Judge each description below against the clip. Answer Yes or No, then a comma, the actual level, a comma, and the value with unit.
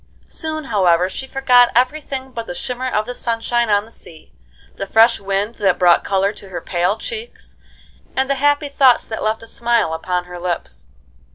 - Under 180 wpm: No, average, 190 wpm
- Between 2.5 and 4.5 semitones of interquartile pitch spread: No, average, 5.2 semitones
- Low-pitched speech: No, high, 225 Hz